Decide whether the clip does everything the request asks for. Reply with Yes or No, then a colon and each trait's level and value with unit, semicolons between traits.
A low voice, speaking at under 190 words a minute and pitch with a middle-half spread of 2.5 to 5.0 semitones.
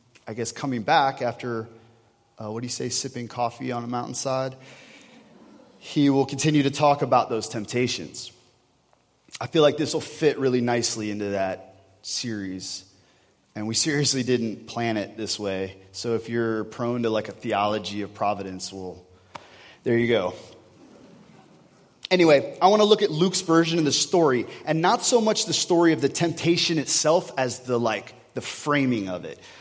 No: low, 125 Hz; average, 170 wpm; wide, 5.5 semitones